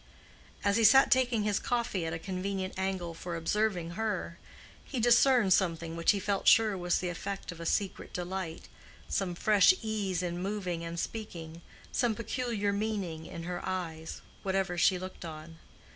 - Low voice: No, high, 190 Hz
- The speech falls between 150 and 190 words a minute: Yes, average, 160 wpm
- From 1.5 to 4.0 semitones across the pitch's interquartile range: Yes, average, 3.7 semitones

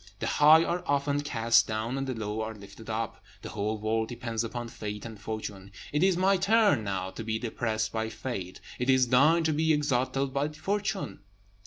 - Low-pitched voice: Yes, low, 120 Hz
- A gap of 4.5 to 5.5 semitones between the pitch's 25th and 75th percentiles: Yes, average, 5.2 semitones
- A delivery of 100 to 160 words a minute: No, average, 195 wpm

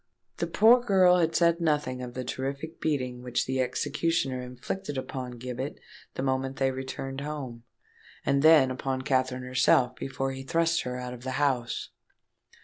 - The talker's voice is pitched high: No, low, 135 Hz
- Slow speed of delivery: No, average, 160 wpm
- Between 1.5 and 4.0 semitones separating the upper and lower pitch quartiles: Yes, average, 2.9 semitones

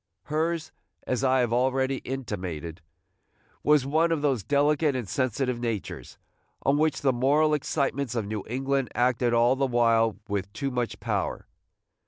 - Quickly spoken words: No, average, 150 wpm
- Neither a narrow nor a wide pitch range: Yes, average, 3.3 semitones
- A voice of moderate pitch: No, low, 130 Hz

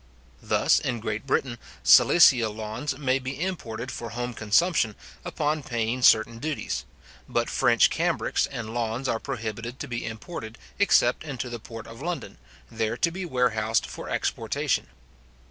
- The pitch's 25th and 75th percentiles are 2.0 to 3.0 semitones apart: No, average, 3.5 semitones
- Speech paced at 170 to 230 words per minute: No, average, 145 wpm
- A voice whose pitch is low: Yes, low, 120 Hz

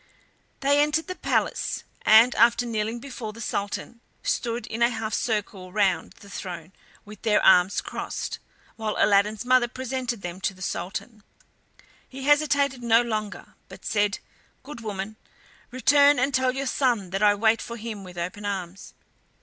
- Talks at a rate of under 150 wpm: No, average, 160 wpm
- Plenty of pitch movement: No, average, 3.8 semitones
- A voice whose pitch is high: Yes, high, 225 Hz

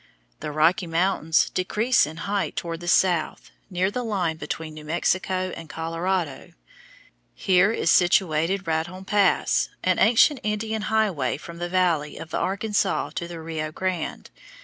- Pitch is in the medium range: Yes, medium, 180 Hz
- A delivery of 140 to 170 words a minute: Yes, average, 150 wpm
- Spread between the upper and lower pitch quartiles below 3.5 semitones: Yes, average, 3.1 semitones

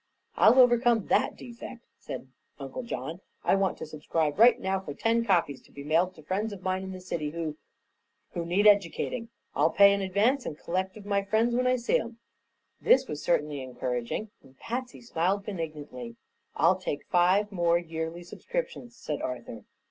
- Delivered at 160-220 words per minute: Yes, average, 180 wpm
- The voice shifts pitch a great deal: Yes, wide, 6.2 semitones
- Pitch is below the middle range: No, high, 190 Hz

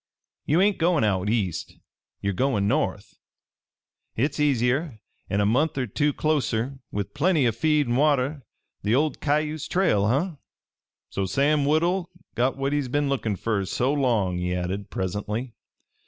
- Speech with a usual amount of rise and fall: No, wide, 6.3 semitones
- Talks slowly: No, average, 155 wpm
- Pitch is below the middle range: Yes, low, 130 Hz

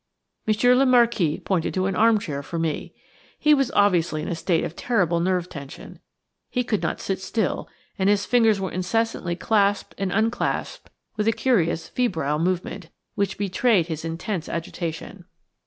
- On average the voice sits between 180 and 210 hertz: Yes, high, 190 Hz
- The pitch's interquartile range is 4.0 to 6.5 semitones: Yes, average, 4.9 semitones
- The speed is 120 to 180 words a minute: Yes, average, 160 wpm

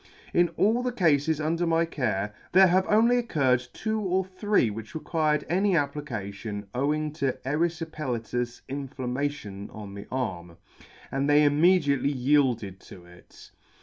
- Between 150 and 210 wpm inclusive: No, average, 140 wpm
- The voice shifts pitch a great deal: Yes, wide, 5.7 semitones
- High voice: No, medium, 145 Hz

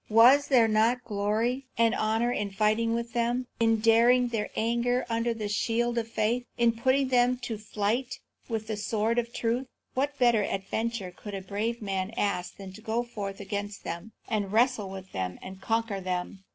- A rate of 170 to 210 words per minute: Yes, average, 180 wpm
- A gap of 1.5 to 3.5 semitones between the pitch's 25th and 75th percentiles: Yes, average, 2.7 semitones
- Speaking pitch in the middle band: No, high, 225 Hz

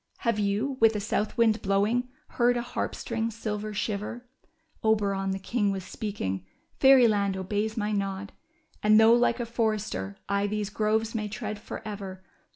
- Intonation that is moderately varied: No, narrow, 2.3 semitones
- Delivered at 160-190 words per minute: Yes, average, 165 wpm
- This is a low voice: No, high, 210 Hz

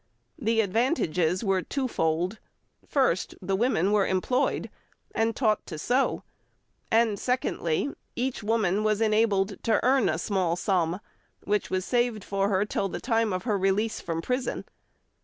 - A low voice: No, high, 210 Hz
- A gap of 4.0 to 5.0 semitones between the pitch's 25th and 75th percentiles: No, average, 3.6 semitones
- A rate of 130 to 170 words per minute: Yes, average, 145 wpm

